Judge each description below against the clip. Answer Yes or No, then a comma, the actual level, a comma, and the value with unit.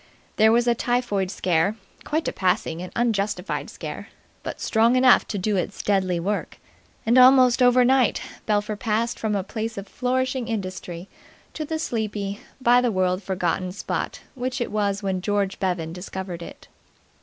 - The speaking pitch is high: Yes, high, 210 Hz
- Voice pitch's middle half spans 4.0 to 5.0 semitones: Yes, average, 4.3 semitones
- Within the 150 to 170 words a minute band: Yes, average, 160 wpm